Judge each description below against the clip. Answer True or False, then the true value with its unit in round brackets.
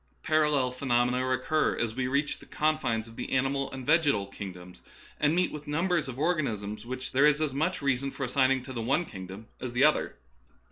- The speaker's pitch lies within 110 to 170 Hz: True (135 Hz)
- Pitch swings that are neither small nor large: True (3.8 semitones)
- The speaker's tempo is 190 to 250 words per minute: True (205 wpm)